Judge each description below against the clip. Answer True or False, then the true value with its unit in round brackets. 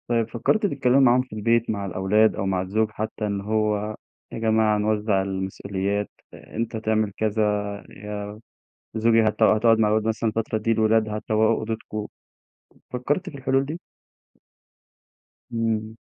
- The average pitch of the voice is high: False (110 Hz)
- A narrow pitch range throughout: True (1.4 semitones)